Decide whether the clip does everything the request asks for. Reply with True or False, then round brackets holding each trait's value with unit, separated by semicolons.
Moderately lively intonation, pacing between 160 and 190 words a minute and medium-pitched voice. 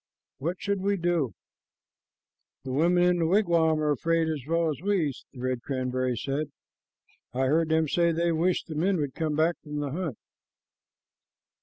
True (3.3 semitones; 170 wpm; 160 Hz)